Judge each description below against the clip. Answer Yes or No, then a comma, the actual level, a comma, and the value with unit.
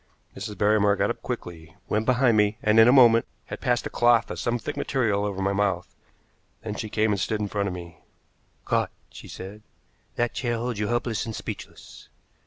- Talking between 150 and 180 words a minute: No, average, 200 wpm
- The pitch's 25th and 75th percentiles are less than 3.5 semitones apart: Yes, average, 2.7 semitones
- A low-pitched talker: Yes, low, 105 Hz